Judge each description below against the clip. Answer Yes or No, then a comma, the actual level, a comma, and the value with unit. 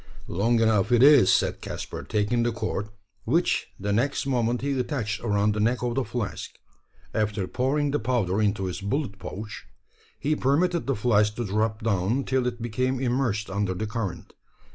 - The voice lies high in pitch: No, low, 115 Hz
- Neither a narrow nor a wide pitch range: Yes, average, 3.6 semitones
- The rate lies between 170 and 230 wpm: Yes, average, 175 wpm